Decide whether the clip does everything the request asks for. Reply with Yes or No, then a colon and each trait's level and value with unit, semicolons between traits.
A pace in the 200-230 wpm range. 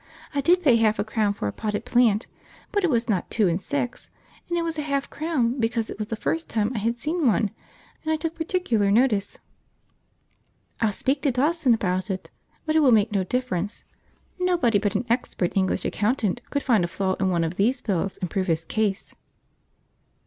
Yes: fast, 205 wpm